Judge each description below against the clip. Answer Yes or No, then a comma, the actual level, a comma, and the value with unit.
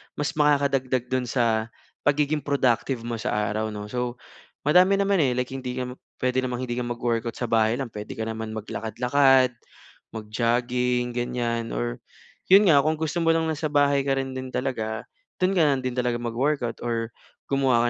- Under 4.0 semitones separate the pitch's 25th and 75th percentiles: Yes, average, 3.1 semitones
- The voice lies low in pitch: Yes, low, 125 Hz